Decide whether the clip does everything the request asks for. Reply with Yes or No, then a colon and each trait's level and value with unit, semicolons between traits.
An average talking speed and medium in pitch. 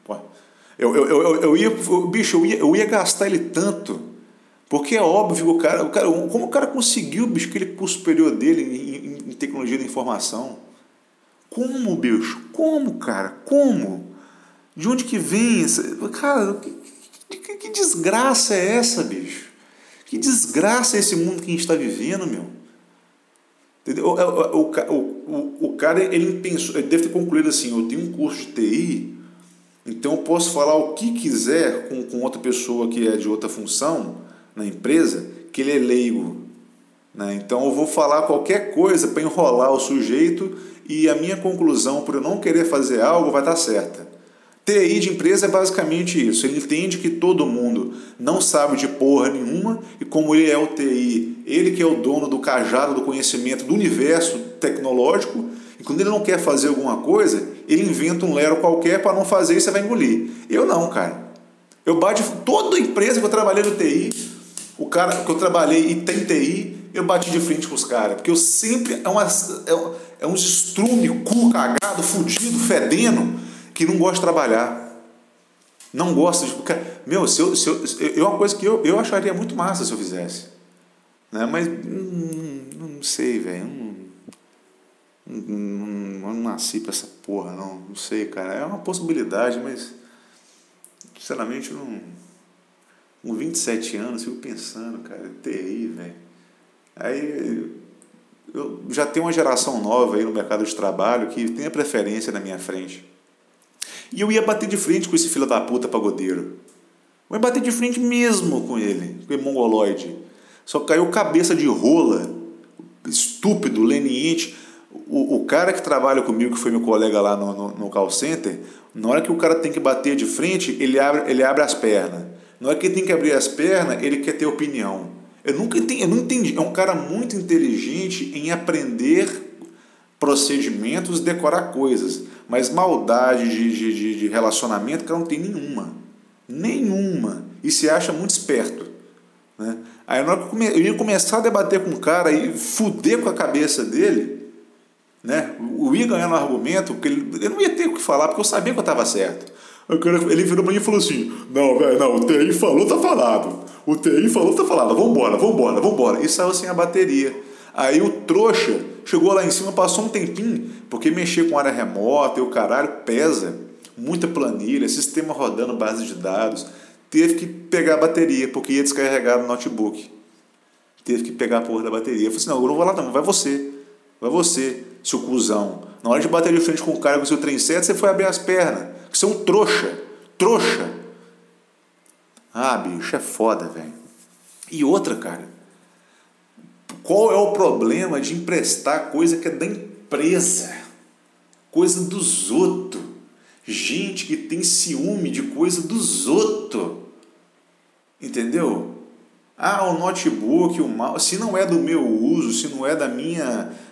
Yes: average, 180 wpm; medium, 175 Hz